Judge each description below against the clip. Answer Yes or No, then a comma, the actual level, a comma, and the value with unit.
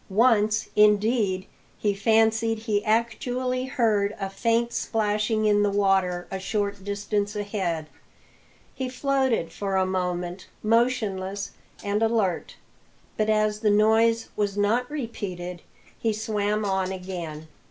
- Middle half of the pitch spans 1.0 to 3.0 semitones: Yes, narrow, 2.6 semitones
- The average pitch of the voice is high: Yes, high, 210 Hz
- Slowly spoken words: Yes, slow, 120 wpm